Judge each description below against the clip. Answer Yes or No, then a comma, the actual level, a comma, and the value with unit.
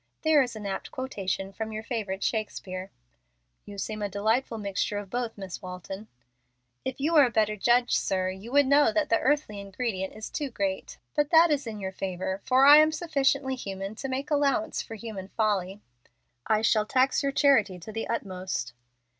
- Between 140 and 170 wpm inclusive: No, average, 190 wpm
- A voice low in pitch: No, high, 220 Hz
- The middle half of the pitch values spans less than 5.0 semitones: No, wide, 5.4 semitones